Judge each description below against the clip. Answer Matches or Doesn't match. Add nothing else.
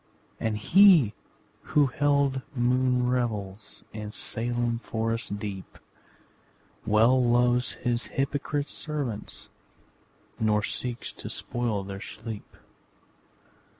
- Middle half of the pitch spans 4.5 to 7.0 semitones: Doesn't match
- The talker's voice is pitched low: Matches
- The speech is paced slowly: Matches